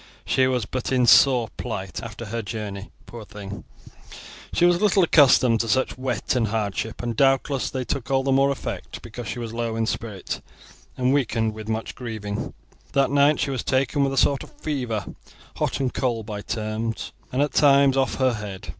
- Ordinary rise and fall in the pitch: Yes, average, 3.5 semitones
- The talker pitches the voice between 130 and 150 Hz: No, low, 120 Hz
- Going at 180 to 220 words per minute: Yes, average, 190 wpm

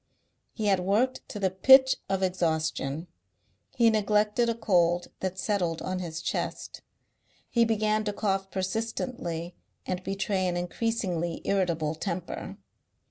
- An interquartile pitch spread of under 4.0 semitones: Yes, average, 3.6 semitones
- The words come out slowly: Yes, slow, 130 wpm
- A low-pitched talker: No, high, 190 Hz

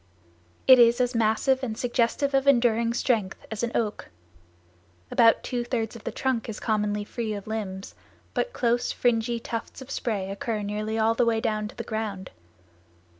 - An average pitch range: No, narrow, 2.1 semitones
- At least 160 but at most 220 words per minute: Yes, average, 175 wpm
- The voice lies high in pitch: Yes, high, 230 Hz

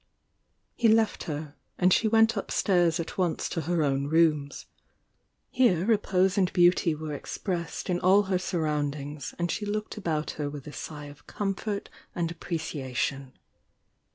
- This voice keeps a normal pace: Yes, average, 150 wpm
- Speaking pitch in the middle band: Yes, medium, 170 Hz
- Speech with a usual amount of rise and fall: Yes, average, 4.5 semitones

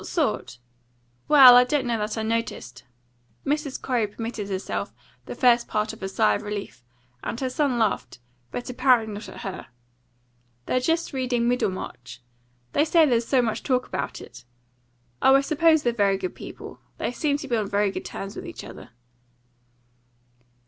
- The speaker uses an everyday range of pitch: Yes, average, 4.3 semitones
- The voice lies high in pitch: Yes, high, 235 Hz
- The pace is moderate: Yes, average, 175 wpm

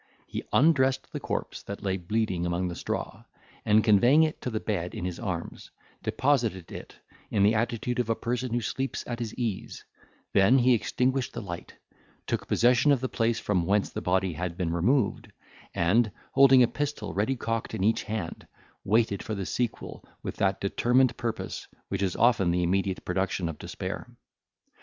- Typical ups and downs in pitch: Yes, average, 4.6 semitones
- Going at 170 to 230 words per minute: Yes, average, 180 wpm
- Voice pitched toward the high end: No, low, 110 Hz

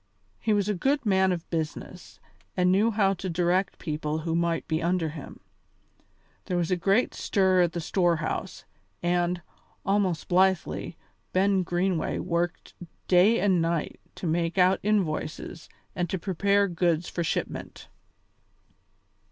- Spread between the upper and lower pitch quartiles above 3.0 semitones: No, narrow, 2.4 semitones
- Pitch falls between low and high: Yes, medium, 180 Hz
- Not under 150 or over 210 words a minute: No, average, 140 wpm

